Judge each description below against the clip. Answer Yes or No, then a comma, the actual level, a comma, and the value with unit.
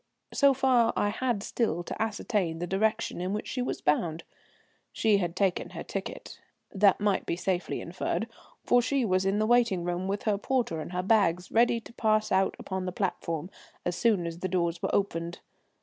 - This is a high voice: Yes, high, 195 Hz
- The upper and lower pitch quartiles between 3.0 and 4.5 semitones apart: Yes, average, 4.0 semitones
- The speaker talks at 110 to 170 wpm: No, average, 195 wpm